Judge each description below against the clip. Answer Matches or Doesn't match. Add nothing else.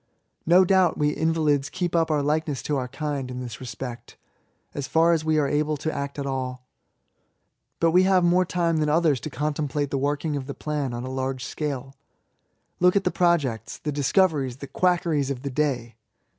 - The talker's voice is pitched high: Doesn't match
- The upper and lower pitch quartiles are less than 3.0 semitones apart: Doesn't match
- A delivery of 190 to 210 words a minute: Matches